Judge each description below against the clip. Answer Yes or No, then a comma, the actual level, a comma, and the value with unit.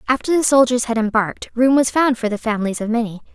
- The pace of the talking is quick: Yes, fast, 235 wpm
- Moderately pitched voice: No, high, 240 Hz